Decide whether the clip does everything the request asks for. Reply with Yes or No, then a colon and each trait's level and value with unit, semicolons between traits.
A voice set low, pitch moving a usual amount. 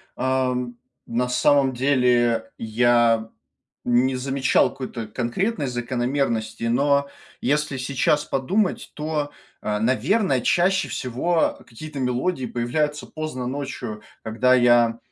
Yes: low, 130 Hz; average, 3.1 semitones